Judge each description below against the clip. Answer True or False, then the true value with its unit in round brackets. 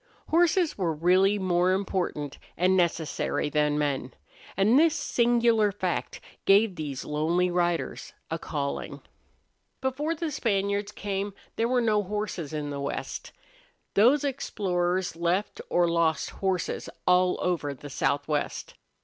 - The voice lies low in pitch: False (185 Hz)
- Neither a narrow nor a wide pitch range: True (4.5 semitones)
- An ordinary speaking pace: False (125 wpm)